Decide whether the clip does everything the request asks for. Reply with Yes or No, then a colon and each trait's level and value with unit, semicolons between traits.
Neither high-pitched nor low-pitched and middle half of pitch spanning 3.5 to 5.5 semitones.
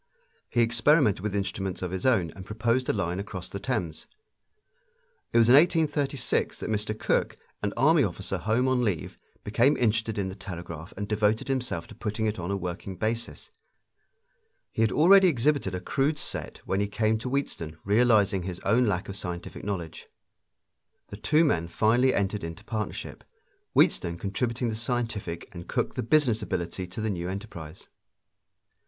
No: low, 105 Hz; average, 4.5 semitones